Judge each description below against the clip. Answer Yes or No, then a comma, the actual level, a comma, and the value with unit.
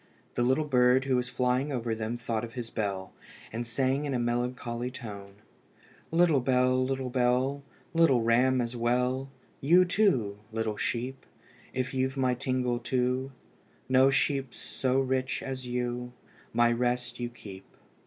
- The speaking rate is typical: Yes, average, 150 wpm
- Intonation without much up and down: Yes, narrow, 1.8 semitones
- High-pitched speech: No, low, 125 Hz